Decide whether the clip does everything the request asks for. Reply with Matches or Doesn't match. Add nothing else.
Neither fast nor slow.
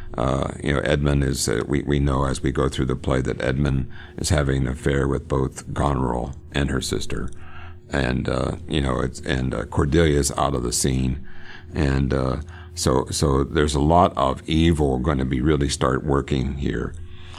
Matches